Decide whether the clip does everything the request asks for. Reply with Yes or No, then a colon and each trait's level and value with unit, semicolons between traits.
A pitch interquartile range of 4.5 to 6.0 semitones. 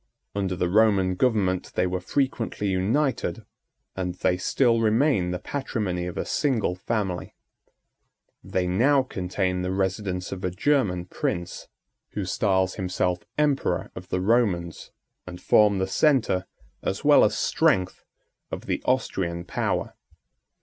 No: average, 3.9 semitones